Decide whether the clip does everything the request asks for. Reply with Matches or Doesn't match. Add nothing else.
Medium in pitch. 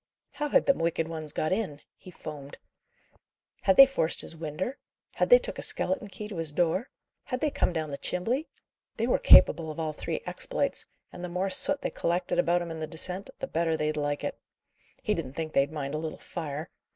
Matches